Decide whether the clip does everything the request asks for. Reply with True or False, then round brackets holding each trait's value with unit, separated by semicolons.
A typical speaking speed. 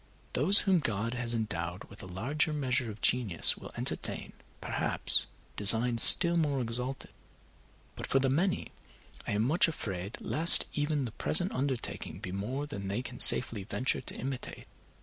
True (160 wpm)